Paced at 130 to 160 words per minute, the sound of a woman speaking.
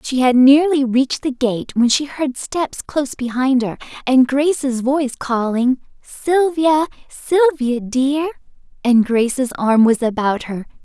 Yes: average, 145 wpm; female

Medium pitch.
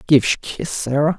Yes: medium, 145 Hz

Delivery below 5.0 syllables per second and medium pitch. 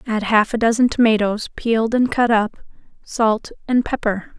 No: 4.7 syllables/s; high, 225 Hz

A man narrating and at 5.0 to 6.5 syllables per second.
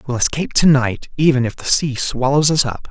Yes: male; 5.5 syllables/s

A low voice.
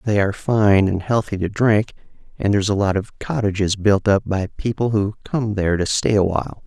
Yes: low, 100 Hz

